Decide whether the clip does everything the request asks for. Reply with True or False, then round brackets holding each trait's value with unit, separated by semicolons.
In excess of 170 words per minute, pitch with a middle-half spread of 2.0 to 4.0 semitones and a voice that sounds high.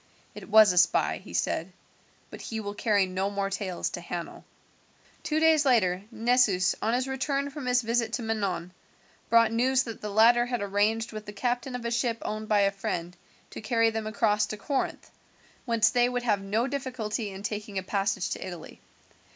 True (190 wpm; 3.4 semitones; 220 Hz)